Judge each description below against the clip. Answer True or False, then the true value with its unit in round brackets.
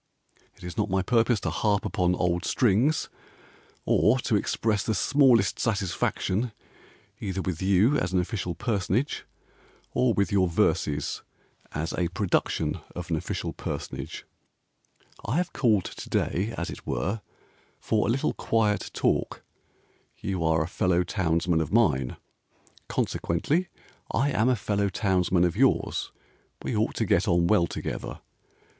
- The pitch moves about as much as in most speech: True (4.3 semitones)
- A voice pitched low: True (95 Hz)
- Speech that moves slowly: False (145 wpm)